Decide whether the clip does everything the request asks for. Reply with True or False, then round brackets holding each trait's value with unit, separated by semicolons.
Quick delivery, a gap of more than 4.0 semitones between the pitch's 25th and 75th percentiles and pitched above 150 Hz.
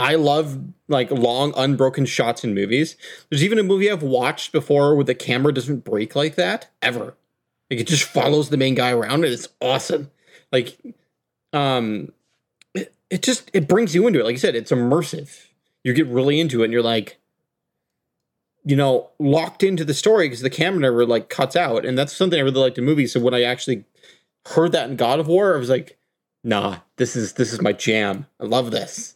False (210 wpm; 4.4 semitones; 140 Hz)